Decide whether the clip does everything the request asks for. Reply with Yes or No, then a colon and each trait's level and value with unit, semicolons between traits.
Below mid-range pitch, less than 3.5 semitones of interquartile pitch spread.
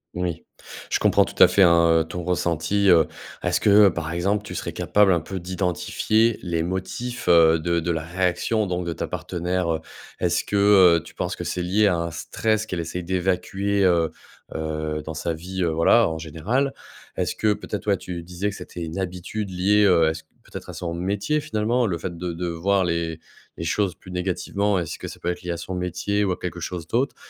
Yes: very low, 90 Hz; average, 3.0 semitones